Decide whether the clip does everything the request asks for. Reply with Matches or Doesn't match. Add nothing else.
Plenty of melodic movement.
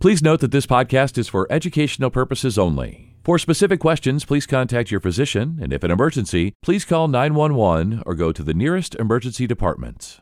Matches